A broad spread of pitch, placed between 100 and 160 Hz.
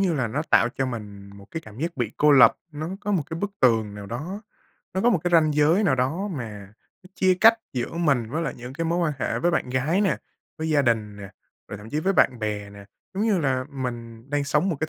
Yes: wide, 6.5 semitones; medium, 140 Hz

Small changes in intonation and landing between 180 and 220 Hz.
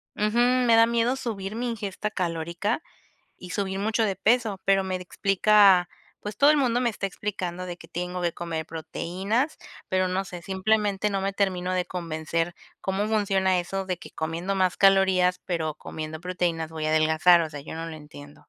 No: average, 3.4 semitones; high, 190 Hz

